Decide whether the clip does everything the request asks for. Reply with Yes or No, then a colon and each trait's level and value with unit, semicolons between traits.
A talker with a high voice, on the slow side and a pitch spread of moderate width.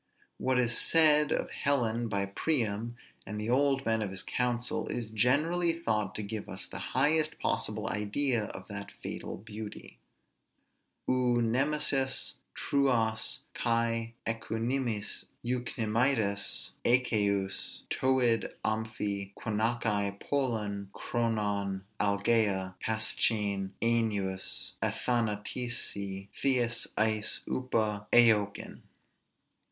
No: low, 115 Hz; slow, 95 wpm; average, 3.1 semitones